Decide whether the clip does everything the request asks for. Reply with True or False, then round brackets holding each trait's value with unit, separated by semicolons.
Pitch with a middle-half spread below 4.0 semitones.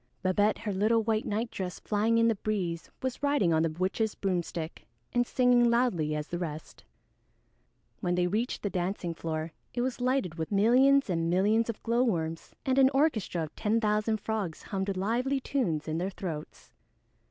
False (5.2 semitones)